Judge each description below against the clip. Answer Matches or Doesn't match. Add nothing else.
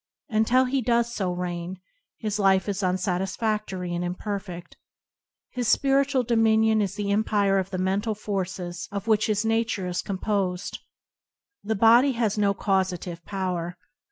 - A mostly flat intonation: Doesn't match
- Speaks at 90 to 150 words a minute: Matches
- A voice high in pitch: Matches